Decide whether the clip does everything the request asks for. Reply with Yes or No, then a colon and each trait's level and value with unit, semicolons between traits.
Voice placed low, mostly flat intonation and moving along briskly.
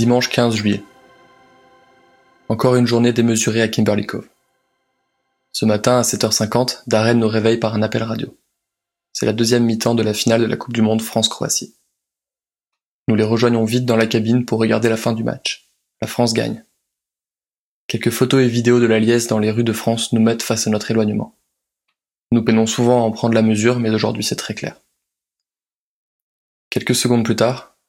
No: low, 115 Hz; narrow, 1.3 semitones; average, 185 wpm